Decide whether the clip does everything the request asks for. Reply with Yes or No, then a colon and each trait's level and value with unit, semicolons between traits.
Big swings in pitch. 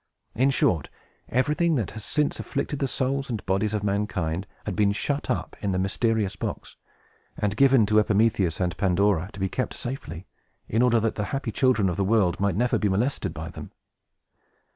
No: average, 4.4 semitones